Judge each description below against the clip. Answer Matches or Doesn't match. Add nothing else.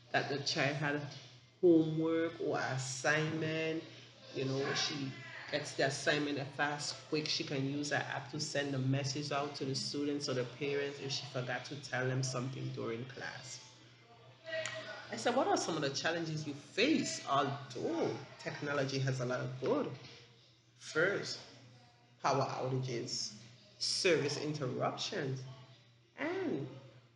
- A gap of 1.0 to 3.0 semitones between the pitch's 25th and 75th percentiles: Matches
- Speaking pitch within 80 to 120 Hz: Doesn't match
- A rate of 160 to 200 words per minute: Doesn't match